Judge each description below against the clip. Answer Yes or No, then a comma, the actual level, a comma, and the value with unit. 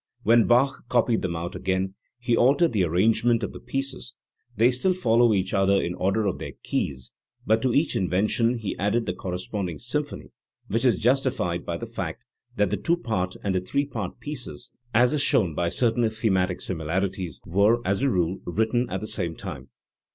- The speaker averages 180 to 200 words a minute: Yes, average, 190 wpm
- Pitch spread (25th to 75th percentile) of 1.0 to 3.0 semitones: No, average, 4.7 semitones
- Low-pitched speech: Yes, low, 105 Hz